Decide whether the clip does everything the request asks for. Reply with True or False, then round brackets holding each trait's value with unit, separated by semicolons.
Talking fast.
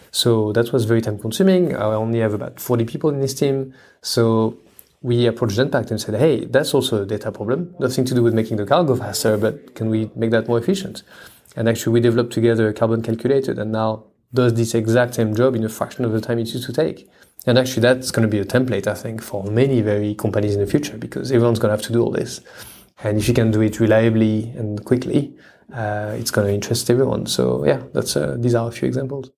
True (240 wpm)